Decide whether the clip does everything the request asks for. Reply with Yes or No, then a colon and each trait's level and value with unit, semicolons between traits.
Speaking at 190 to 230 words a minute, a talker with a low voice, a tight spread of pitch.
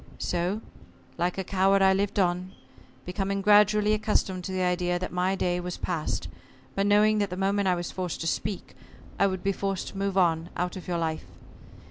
No: average, 195 wpm; high, 190 Hz; narrow, 1.8 semitones